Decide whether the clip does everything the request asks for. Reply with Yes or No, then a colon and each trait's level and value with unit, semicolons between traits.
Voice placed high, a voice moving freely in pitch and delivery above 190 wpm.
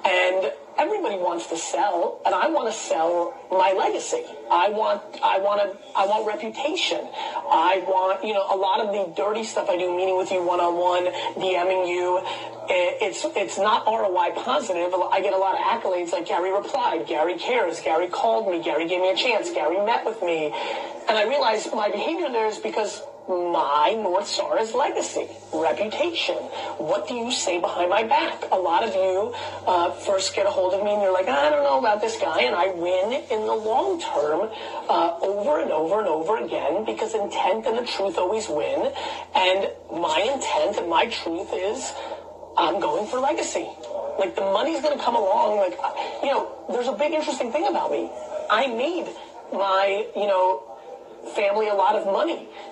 No: high, 205 Hz; wide, 7.6 semitones; average, 185 wpm